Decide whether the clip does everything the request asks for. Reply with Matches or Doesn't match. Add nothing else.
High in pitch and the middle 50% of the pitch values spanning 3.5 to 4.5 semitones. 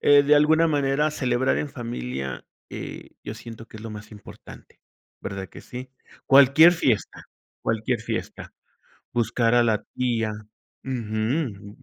Doesn't match